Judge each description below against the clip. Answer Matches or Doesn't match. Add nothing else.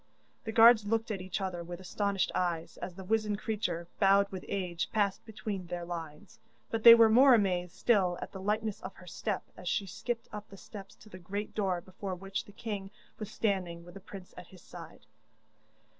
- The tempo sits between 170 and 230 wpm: Matches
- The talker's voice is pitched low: Doesn't match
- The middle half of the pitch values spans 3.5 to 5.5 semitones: Doesn't match